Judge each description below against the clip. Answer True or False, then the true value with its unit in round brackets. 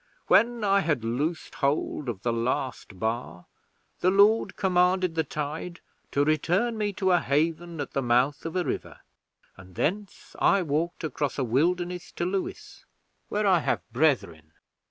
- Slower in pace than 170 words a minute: True (155 wpm)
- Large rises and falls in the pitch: True (6.2 semitones)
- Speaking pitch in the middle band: True (160 Hz)